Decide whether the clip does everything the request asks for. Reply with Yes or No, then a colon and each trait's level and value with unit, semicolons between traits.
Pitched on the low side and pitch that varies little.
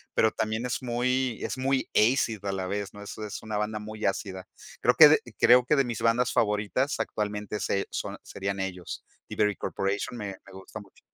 No: low, 105 Hz; average, 3.1 semitones